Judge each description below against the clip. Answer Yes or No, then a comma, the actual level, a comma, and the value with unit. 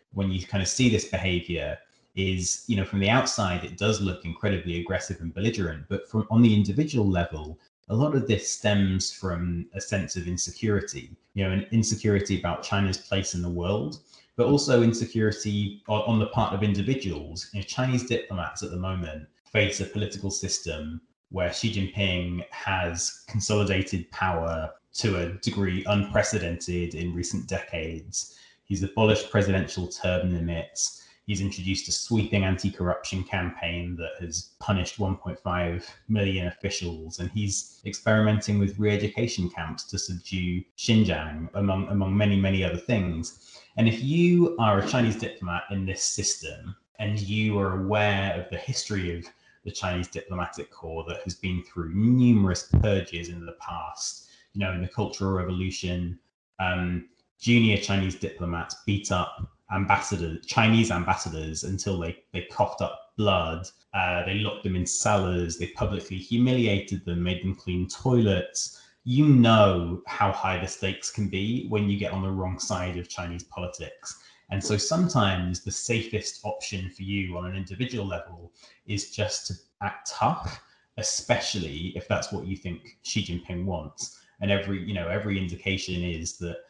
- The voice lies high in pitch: No, very low, 95 Hz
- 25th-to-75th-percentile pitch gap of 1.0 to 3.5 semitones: Yes, average, 2.9 semitones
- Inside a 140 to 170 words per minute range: Yes, average, 160 wpm